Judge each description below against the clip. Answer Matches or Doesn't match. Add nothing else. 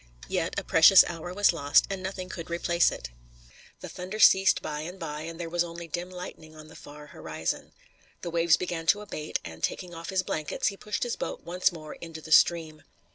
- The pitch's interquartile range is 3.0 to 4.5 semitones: Doesn't match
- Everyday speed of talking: Doesn't match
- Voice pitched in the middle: Matches